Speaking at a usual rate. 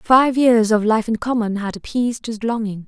No: fast, 210 wpm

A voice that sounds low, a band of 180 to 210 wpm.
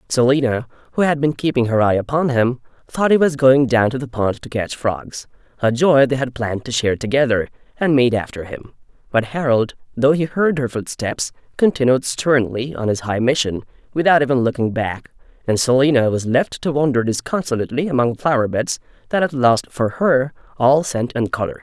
Yes: low, 130 Hz; average, 185 wpm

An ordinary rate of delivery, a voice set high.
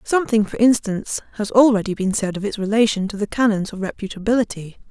Yes: average, 185 wpm; high, 210 Hz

